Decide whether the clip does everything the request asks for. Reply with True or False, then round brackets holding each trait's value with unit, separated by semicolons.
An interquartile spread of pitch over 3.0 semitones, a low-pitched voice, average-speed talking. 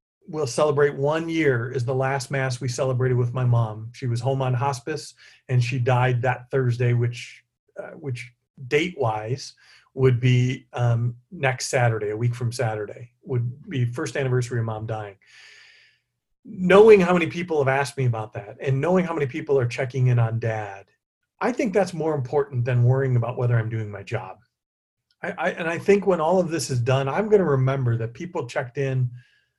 True (3.7 semitones; 130 Hz; 190 wpm)